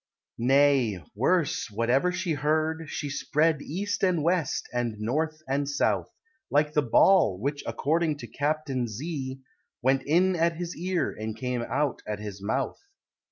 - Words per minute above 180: No, average, 150 wpm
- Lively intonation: No, average, 4.3 semitones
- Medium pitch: Yes, medium, 145 Hz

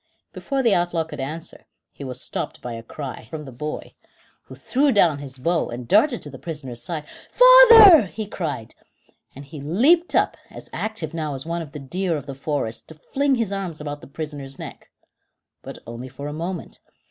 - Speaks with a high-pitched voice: No, medium, 155 Hz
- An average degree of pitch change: No, wide, 6.1 semitones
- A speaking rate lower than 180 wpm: No, average, 195 wpm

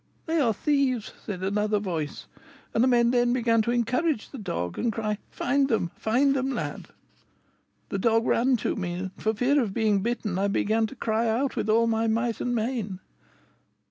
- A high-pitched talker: Yes, high, 225 Hz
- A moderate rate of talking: Yes, average, 190 wpm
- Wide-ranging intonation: No, average, 2.7 semitones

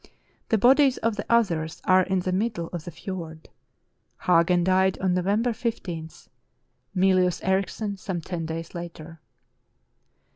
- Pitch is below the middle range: No, medium, 185 Hz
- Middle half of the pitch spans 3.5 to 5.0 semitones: No, average, 3.1 semitones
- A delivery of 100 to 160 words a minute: Yes, average, 145 wpm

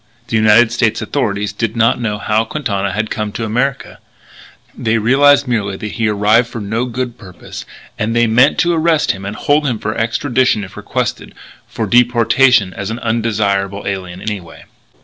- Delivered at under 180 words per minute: Yes, average, 170 wpm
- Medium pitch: No, low, 110 Hz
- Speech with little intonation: No, average, 3.0 semitones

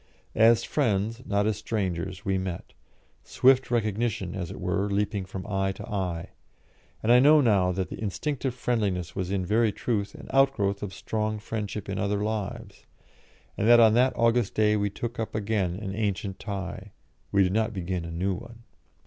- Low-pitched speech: Yes, low, 105 Hz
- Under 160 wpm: No, average, 180 wpm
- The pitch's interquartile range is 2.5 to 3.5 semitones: Yes, average, 2.9 semitones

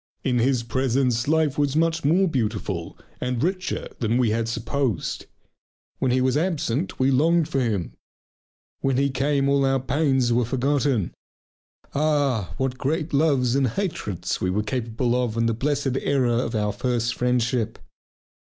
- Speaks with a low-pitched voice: Yes, low, 130 Hz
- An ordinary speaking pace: Yes, average, 155 wpm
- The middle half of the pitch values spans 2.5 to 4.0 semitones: Yes, average, 3.4 semitones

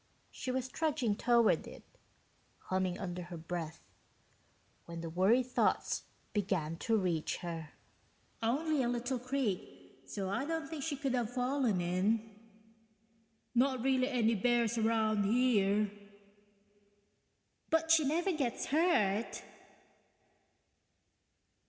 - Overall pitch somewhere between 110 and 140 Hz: No, high, 230 Hz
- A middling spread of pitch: No, wide, 5.7 semitones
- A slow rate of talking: Yes, slow, 115 wpm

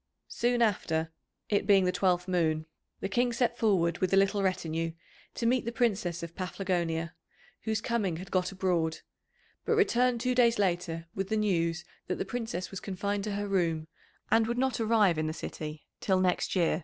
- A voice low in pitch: No, high, 190 Hz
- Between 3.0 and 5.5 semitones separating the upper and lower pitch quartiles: Yes, average, 4.6 semitones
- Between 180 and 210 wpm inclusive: Yes, average, 185 wpm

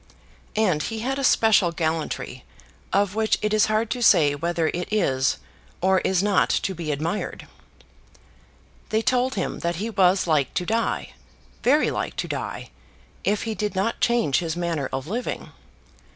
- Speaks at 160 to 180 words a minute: Yes, average, 165 wpm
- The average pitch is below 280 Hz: Yes, high, 190 Hz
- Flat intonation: No, average, 4.9 semitones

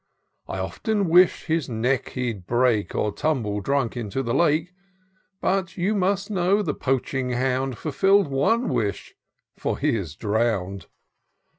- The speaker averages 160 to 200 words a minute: No, average, 145 wpm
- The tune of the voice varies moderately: No, wide, 7.9 semitones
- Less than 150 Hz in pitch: Yes, low, 135 Hz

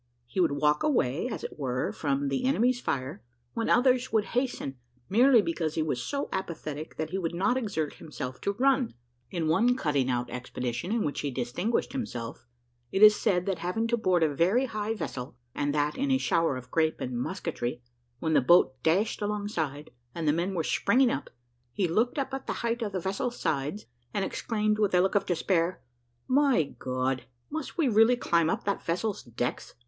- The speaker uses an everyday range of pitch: No, wide, 7.6 semitones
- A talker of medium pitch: Yes, medium, 180 Hz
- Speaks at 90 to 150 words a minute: No, average, 195 wpm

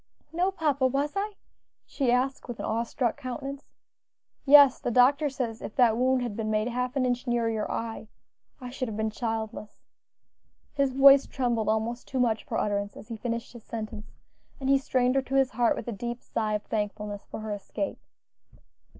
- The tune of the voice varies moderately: Yes, average, 3.4 semitones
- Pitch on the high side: Yes, high, 245 Hz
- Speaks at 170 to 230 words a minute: Yes, average, 195 wpm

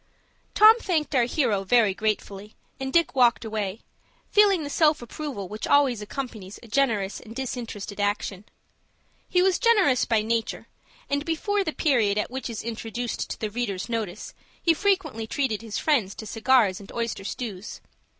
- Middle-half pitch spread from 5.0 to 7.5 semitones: Yes, wide, 5.4 semitones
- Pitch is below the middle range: No, high, 235 Hz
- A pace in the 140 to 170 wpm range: Yes, average, 165 wpm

